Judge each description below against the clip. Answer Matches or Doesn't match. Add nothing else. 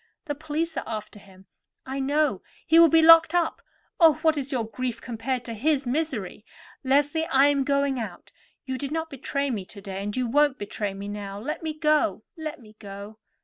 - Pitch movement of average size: Doesn't match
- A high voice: Matches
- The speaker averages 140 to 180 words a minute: Doesn't match